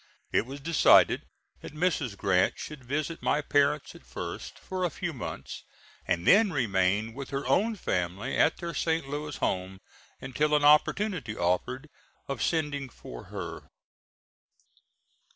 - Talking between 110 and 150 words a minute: Yes, average, 140 wpm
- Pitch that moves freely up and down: Yes, wide, 6.0 semitones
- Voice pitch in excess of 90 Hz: Yes, medium, 140 Hz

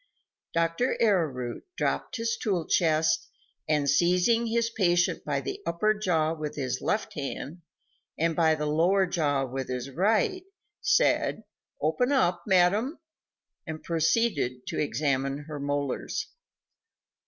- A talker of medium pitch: Yes, medium, 165 Hz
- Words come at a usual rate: No, slow, 120 wpm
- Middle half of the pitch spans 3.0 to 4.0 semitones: No, wide, 5.6 semitones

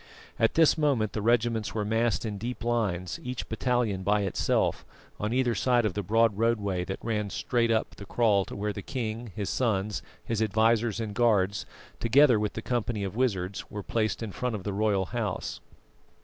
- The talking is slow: No, average, 190 wpm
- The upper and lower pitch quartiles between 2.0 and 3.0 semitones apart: Yes, average, 2.7 semitones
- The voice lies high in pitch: No, low, 110 Hz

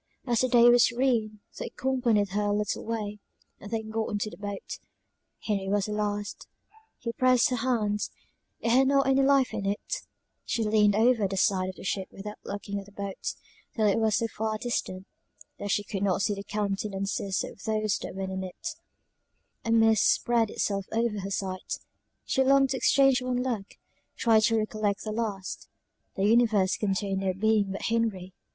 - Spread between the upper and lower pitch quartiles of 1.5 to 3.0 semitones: Yes, average, 2.7 semitones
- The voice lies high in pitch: Yes, high, 210 Hz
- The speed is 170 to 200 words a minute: Yes, average, 185 wpm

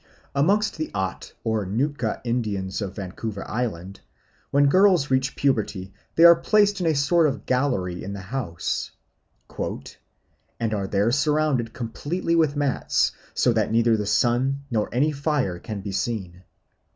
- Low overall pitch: Yes, low, 120 Hz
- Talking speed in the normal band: Yes, average, 150 wpm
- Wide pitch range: Yes, wide, 6.3 semitones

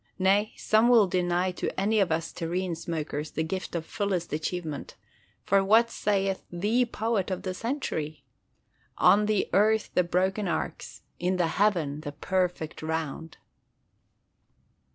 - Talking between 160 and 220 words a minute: No, average, 140 wpm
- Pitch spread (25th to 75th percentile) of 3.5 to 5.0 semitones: Yes, average, 3.9 semitones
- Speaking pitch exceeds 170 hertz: Yes, medium, 185 Hz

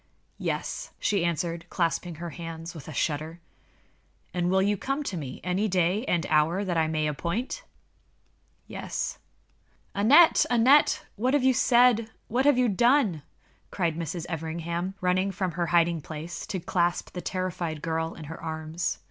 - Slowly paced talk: No, average, 155 wpm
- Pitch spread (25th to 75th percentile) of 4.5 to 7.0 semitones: No, average, 3.9 semitones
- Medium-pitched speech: Yes, medium, 175 Hz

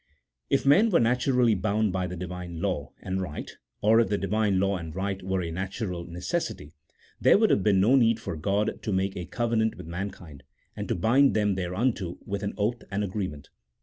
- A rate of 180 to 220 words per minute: Yes, average, 200 wpm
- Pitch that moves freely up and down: No, average, 3.6 semitones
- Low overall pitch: Yes, low, 100 Hz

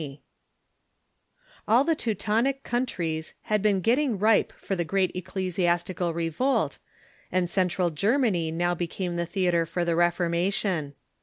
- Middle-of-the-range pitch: Yes, medium, 180 Hz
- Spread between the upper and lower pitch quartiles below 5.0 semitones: Yes, average, 3.7 semitones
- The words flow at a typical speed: No, slow, 130 wpm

